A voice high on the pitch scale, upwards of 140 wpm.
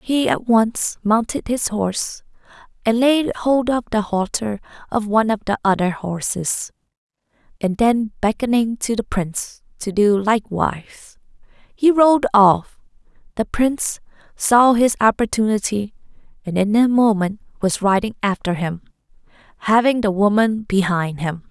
No: high, 215 Hz; slow, 135 wpm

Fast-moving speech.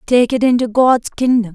No: average, 195 wpm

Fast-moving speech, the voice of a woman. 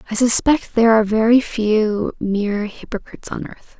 No: average, 160 wpm; female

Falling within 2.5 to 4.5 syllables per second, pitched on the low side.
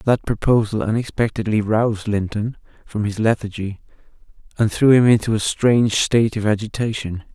No: 5.4 syllables/s; low, 110 Hz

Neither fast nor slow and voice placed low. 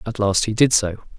No: fast, 255 wpm; low, 105 Hz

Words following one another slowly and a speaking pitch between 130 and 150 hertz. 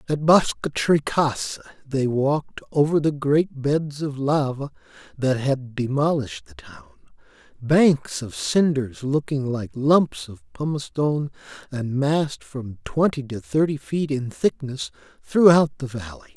Yes: slow, 130 wpm; medium, 140 Hz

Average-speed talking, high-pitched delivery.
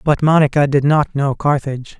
No: average, 180 wpm; medium, 140 Hz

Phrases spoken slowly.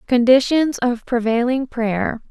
Yes: slow, 105 wpm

